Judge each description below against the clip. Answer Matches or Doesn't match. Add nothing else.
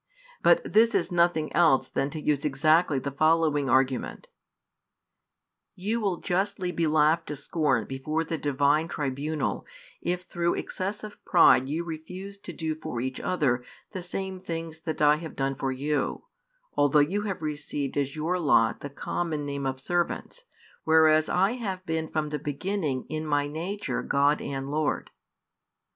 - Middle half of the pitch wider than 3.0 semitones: Matches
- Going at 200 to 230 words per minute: Doesn't match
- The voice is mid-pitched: Matches